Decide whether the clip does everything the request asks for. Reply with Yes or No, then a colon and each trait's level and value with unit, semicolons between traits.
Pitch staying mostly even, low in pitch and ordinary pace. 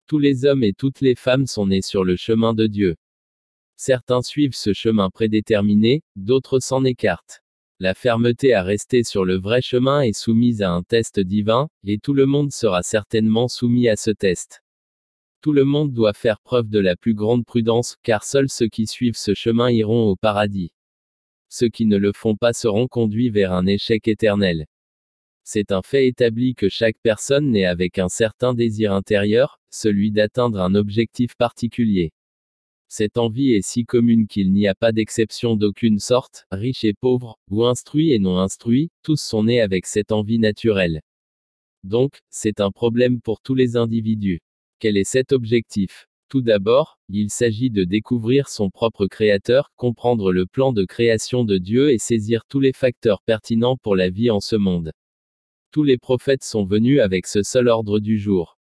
No: average, 3.5 semitones; low, 110 Hz; average, 180 wpm